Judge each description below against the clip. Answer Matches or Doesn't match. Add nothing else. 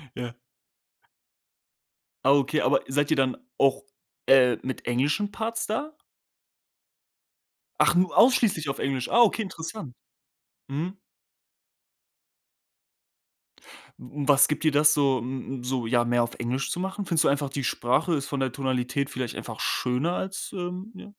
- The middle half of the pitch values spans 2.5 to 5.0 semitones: Doesn't match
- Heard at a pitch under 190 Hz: Matches